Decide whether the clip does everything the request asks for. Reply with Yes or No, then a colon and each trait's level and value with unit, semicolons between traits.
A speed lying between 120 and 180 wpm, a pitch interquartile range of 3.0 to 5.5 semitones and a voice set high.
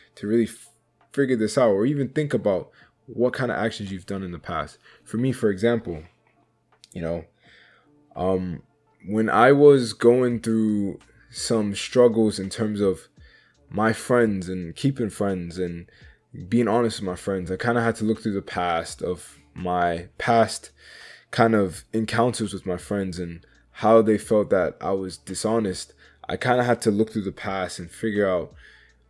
No: average, 175 wpm; average, 3.9 semitones; low, 110 Hz